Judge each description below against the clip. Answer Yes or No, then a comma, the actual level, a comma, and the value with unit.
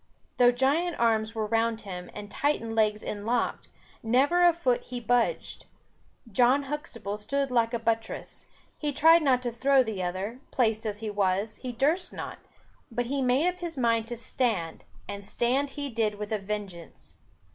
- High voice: Yes, high, 235 Hz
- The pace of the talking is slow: No, average, 170 wpm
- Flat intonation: No, average, 4.1 semitones